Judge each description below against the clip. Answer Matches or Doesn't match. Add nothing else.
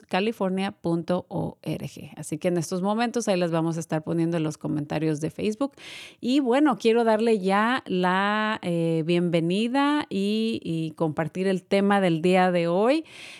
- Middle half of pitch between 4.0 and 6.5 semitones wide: Matches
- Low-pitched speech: Doesn't match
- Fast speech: Doesn't match